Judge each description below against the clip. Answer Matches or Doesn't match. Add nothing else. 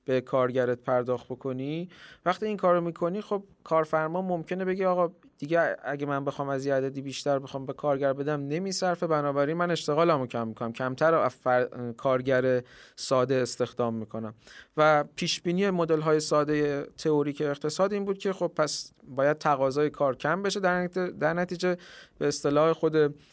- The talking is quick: Matches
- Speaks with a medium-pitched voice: Matches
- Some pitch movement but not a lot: Matches